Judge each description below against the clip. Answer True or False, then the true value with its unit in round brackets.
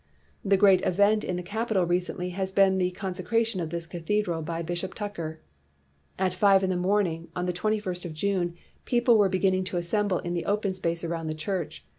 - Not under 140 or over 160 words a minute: False (205 wpm)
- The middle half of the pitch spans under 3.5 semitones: True (2.6 semitones)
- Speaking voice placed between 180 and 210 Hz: True (185 Hz)